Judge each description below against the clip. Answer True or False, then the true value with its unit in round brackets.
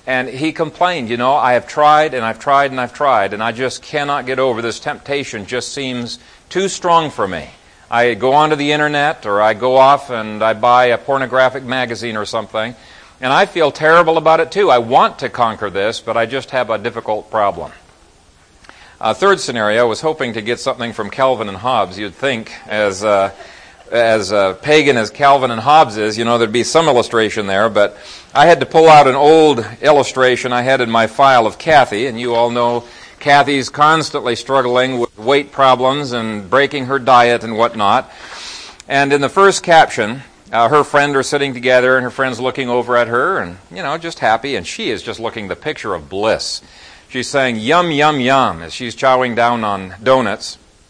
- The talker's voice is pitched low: True (130 Hz)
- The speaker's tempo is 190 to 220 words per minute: True (200 wpm)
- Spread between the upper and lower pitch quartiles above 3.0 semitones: True (3.4 semitones)